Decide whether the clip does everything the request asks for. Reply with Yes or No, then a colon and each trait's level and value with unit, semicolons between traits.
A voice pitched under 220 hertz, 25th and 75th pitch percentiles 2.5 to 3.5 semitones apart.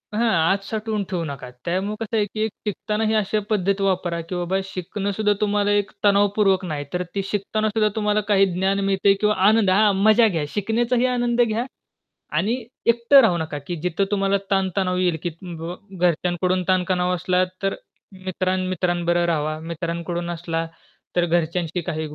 Yes: high, 190 Hz; average, 3.2 semitones